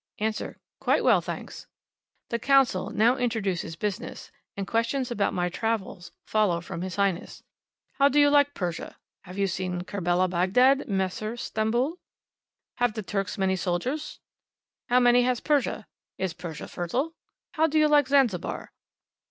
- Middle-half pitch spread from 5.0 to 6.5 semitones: Yes, wide, 5.6 semitones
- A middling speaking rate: Yes, average, 145 wpm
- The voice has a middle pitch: No, high, 215 Hz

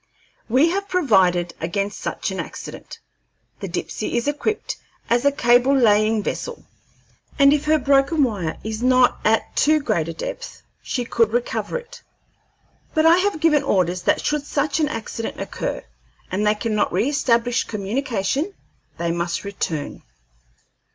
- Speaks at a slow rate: No, average, 145 wpm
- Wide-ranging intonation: Yes, wide, 6.1 semitones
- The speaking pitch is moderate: No, high, 245 Hz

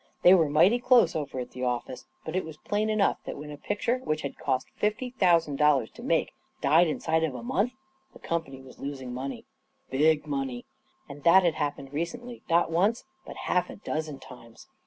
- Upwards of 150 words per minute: Yes, average, 200 wpm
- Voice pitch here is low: No, medium, 155 Hz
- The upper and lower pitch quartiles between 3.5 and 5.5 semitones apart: Yes, average, 5.2 semitones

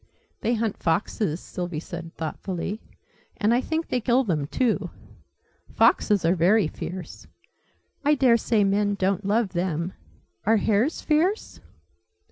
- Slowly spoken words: Yes, slow, 125 wpm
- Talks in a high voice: Yes, high, 205 Hz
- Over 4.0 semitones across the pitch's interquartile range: Yes, average, 5.0 semitones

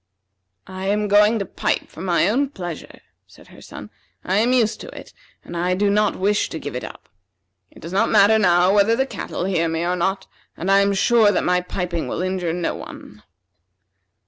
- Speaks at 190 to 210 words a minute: Yes, fast, 205 wpm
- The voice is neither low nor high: No, high, 195 Hz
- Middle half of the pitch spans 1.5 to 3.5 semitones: Yes, average, 2.8 semitones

